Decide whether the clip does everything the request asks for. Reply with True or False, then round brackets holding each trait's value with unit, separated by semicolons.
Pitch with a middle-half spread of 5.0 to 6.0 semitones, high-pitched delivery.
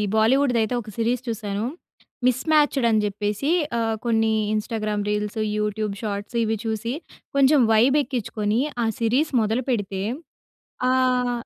False (3.0 semitones; 225 Hz)